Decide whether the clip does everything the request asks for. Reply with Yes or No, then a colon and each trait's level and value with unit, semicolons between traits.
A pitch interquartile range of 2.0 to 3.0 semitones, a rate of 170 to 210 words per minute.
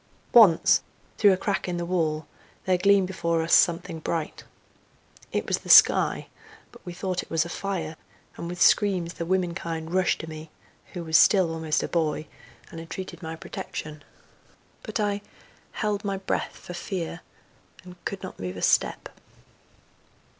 No: narrow, 2.6 semitones; average, 160 wpm